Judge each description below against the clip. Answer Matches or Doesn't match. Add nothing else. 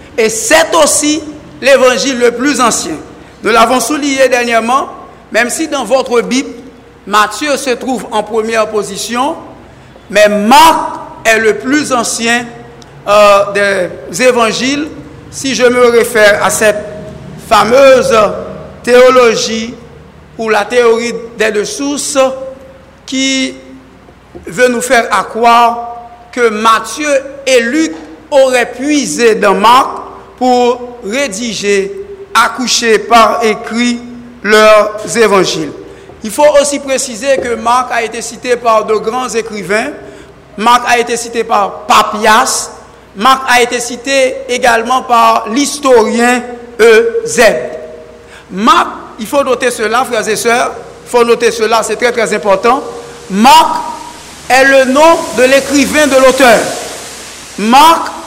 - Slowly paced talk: Matches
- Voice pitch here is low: Doesn't match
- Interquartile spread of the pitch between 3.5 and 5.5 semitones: Doesn't match